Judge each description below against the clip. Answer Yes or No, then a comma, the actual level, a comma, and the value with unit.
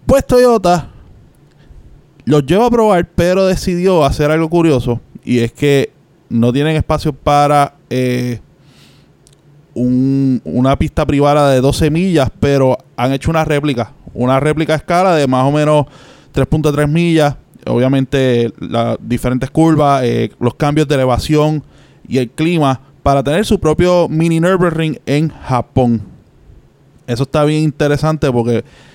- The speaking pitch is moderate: Yes, medium, 145 Hz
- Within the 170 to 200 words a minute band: No, average, 135 wpm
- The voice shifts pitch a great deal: No, average, 3.3 semitones